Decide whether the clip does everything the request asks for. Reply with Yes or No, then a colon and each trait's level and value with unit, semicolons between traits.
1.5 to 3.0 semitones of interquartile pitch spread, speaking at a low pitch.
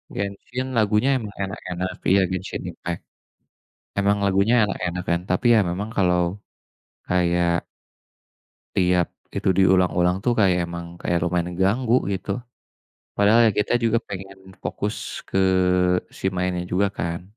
Yes: narrow, 2.4 semitones; very low, 95 Hz